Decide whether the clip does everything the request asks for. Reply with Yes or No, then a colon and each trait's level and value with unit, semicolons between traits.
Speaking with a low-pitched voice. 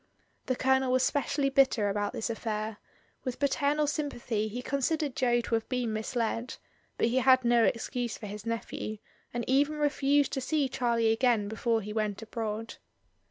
No: high, 240 Hz